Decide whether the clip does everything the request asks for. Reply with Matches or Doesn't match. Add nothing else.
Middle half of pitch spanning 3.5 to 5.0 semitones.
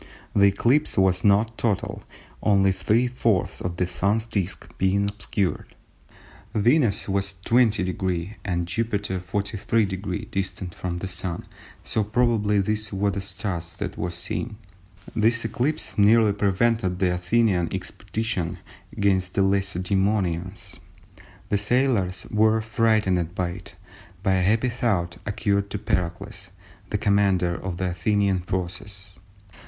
Doesn't match